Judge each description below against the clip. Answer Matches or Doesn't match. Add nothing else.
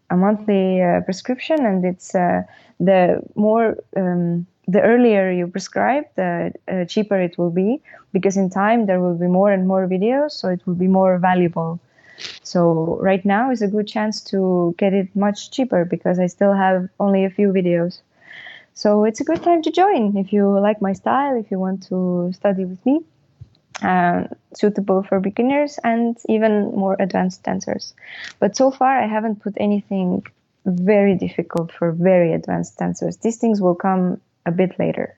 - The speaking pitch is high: Matches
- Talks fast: Doesn't match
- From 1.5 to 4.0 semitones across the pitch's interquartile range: Matches